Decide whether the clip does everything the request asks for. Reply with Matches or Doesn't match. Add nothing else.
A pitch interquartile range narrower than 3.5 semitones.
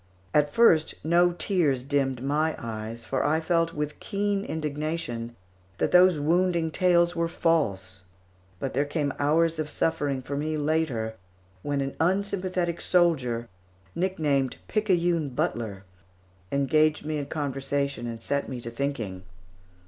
Doesn't match